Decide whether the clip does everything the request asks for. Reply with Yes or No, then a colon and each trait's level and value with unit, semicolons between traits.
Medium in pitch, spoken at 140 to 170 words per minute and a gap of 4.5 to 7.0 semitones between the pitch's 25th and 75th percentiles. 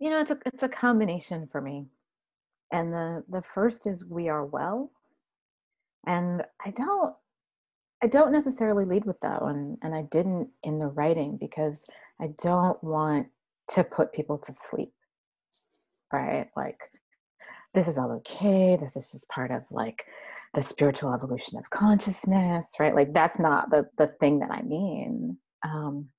Yes: medium, 170 Hz; average, 160 wpm; average, 5.3 semitones